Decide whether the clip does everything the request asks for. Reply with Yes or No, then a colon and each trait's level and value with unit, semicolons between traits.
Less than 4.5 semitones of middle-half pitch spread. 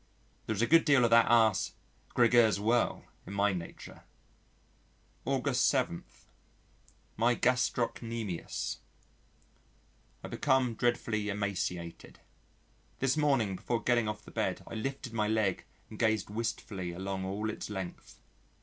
Yes: average, 3.2 semitones